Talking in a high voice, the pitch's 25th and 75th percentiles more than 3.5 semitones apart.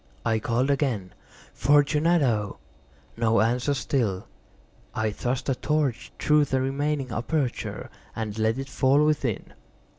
No: low, 130 Hz; average, 4.2 semitones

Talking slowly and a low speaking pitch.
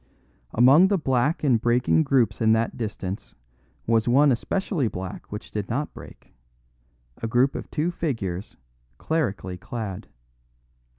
Yes: slow, 130 wpm; low, 120 Hz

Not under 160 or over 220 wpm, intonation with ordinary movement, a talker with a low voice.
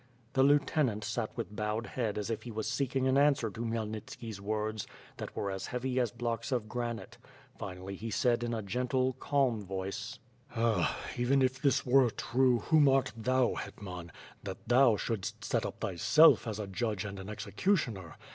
Yes: average, 175 wpm; average, 3.4 semitones; low, 115 Hz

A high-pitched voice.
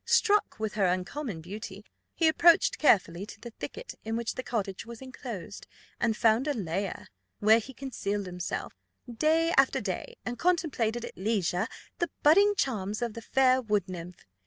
Yes: high, 225 Hz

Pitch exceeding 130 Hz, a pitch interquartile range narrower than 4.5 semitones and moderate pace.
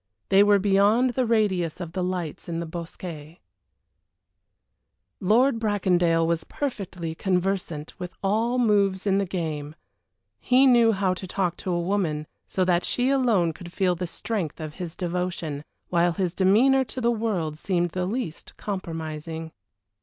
Yes: medium, 185 Hz; average, 3.7 semitones; average, 155 wpm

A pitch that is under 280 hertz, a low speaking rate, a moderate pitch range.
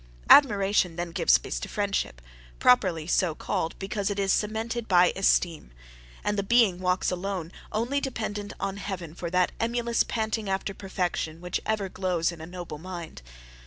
No: high, 190 Hz; average, 160 wpm; average, 3.1 semitones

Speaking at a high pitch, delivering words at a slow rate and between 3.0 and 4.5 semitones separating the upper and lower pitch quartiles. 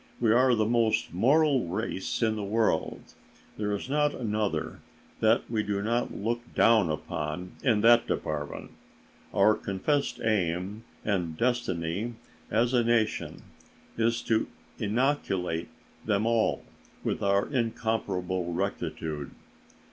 No: low, 110 Hz; slow, 120 wpm; average, 4.0 semitones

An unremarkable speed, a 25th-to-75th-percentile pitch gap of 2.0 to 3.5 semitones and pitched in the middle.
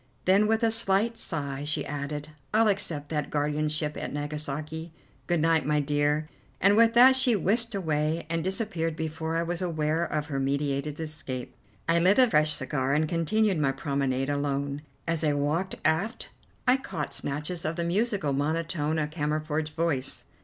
Yes: average, 165 wpm; average, 3.2 semitones; medium, 155 Hz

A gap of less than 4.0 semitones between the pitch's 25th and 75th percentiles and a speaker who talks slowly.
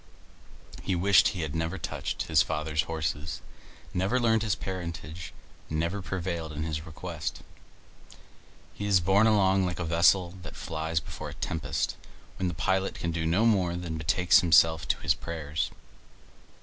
No: average, 2.9 semitones; average, 155 wpm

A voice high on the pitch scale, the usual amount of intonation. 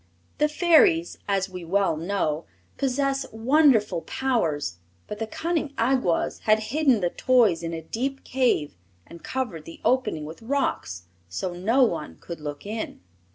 No: high, 215 Hz; wide, 8.0 semitones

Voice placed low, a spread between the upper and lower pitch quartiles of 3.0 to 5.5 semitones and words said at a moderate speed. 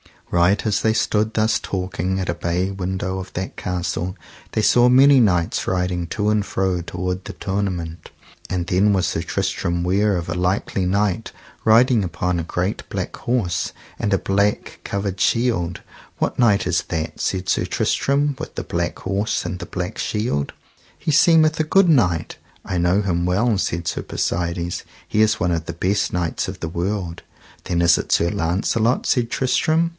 Yes: very low, 95 Hz; average, 3.6 semitones; average, 180 wpm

